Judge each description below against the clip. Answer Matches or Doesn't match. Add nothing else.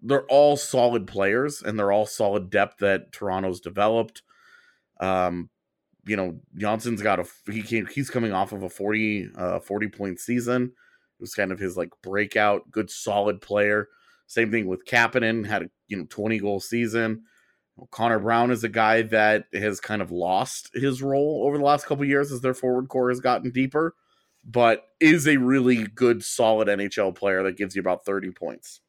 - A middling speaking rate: Matches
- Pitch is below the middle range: Matches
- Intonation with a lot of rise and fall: Doesn't match